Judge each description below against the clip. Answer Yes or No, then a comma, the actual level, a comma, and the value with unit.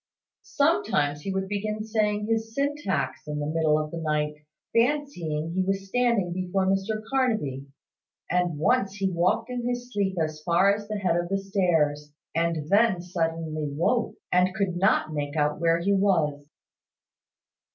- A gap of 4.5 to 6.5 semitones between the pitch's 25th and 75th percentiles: Yes, average, 5.3 semitones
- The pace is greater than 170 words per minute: No, average, 160 wpm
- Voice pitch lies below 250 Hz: Yes, medium, 185 Hz